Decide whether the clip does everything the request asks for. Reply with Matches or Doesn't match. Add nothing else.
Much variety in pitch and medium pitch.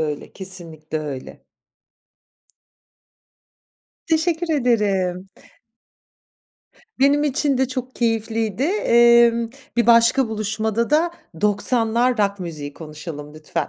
Doesn't match